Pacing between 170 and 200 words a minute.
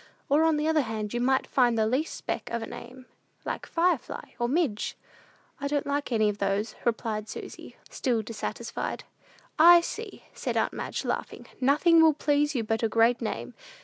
Yes: average, 180 wpm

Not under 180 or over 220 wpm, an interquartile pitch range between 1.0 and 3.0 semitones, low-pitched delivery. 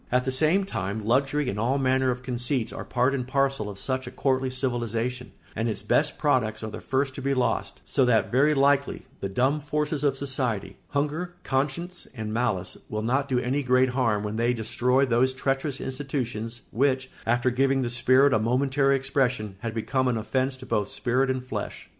Yes: average, 190 wpm; narrow, 2.6 semitones; low, 130 Hz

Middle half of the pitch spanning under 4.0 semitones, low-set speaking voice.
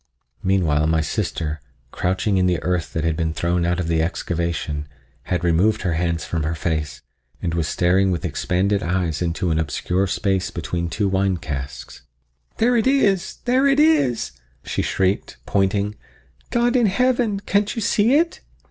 No: average, 5.0 semitones; very low, 90 Hz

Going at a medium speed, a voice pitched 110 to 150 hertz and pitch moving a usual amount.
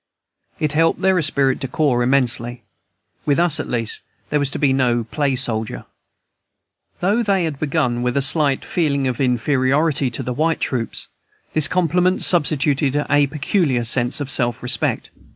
Yes: average, 160 wpm; medium, 140 Hz; average, 3.8 semitones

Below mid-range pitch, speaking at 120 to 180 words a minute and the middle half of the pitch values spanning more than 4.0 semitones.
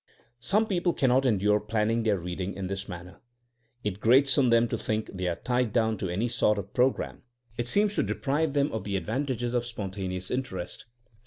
No: low, 110 Hz; average, 200 wpm; average, 4.8 semitones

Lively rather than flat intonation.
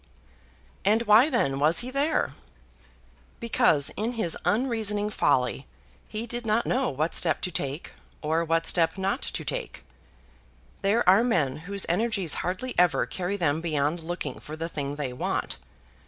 Yes: wide, 6.3 semitones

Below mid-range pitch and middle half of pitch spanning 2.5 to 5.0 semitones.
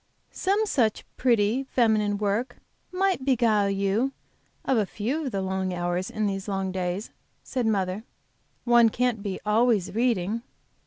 No: high, 215 Hz; average, 4.0 semitones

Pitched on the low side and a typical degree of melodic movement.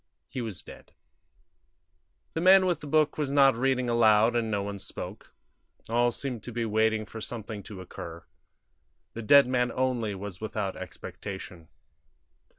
Yes: low, 115 Hz; average, 3.7 semitones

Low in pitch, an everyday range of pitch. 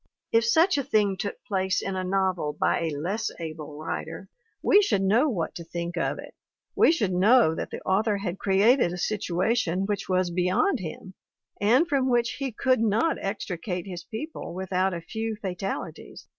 No: high, 195 Hz; average, 4.2 semitones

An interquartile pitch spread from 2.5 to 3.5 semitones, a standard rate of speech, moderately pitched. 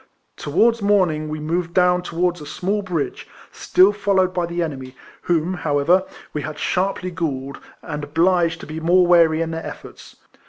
Yes: average, 2.9 semitones; average, 165 wpm; medium, 170 Hz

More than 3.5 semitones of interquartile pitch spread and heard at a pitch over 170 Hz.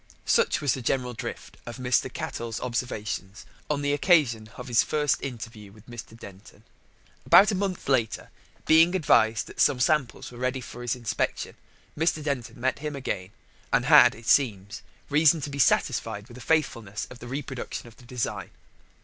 No: average, 4.0 semitones; low, 125 Hz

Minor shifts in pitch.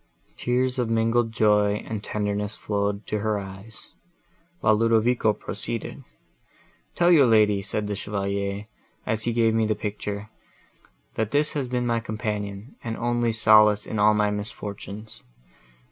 Yes: narrow, 1.8 semitones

